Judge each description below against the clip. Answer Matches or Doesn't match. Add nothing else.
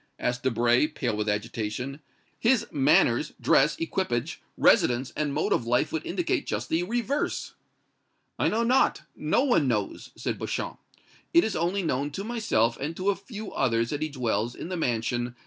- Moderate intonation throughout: Doesn't match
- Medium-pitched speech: Matches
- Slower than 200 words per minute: Matches